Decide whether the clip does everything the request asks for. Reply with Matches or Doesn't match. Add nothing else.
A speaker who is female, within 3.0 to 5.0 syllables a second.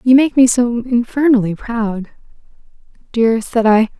Matches